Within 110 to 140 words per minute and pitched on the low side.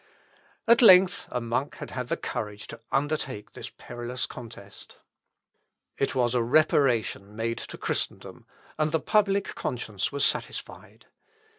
Yes: slow, 135 wpm; low, 125 Hz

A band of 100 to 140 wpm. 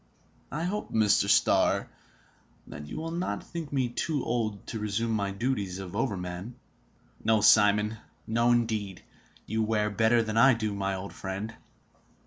No: average, 150 wpm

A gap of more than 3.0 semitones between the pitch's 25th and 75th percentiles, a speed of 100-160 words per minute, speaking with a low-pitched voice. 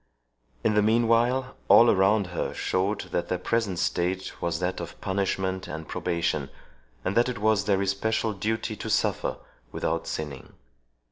Yes: average, 3.5 semitones; average, 150 wpm; very low, 95 Hz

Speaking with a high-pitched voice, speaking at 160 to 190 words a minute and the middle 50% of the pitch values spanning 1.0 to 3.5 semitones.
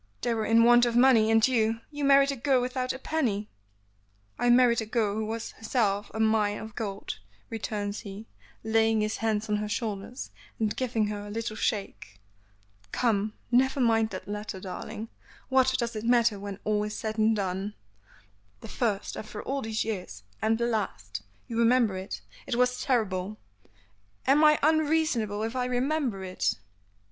Yes: high, 225 Hz; average, 175 wpm; average, 2.8 semitones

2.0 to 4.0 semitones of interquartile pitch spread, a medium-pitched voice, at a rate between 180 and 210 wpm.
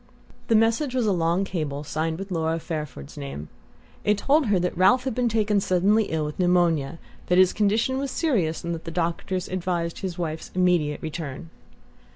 No: average, 4.5 semitones; medium, 180 Hz; average, 185 wpm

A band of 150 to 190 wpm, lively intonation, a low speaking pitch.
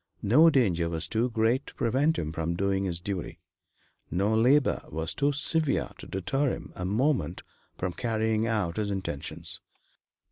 Yes: average, 155 wpm; wide, 6.3 semitones; low, 110 Hz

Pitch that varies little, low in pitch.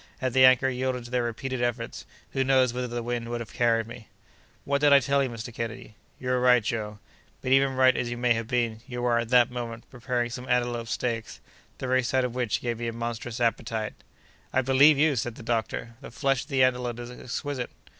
Yes: narrow, 1.7 semitones; low, 120 Hz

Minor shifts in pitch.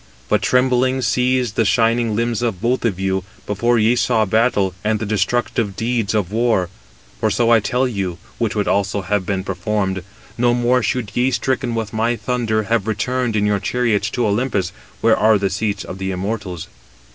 No: average, 3.2 semitones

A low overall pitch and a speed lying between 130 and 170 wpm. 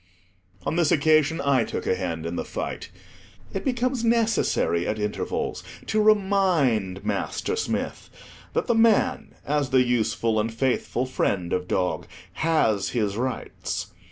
Yes: low, 130 Hz; average, 140 wpm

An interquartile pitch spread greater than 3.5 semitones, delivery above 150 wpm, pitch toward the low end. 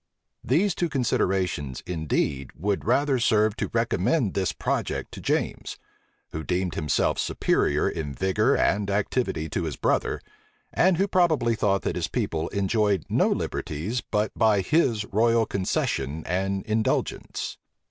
No: average, 4.8 semitones; slow, 135 wpm; low, 100 Hz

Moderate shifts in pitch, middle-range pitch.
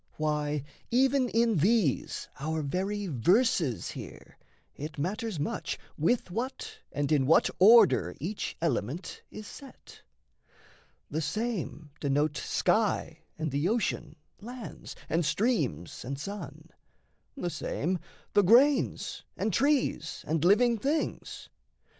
No: wide, 7.4 semitones; medium, 180 Hz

